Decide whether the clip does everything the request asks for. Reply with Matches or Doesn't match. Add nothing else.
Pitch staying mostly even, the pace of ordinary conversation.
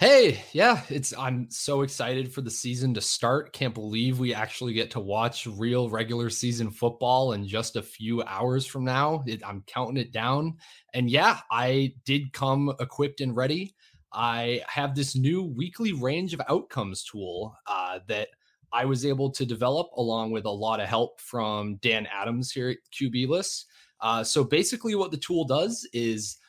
Doesn't match